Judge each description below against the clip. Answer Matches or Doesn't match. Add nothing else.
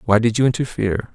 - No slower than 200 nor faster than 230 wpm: Matches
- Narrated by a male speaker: Matches